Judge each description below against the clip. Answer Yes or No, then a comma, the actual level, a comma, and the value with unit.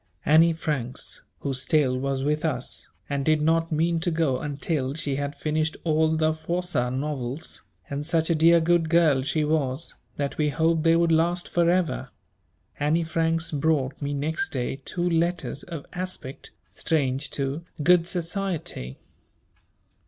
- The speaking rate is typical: Yes, average, 150 wpm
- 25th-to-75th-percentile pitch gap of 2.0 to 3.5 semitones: Yes, average, 2.9 semitones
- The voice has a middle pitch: Yes, medium, 155 Hz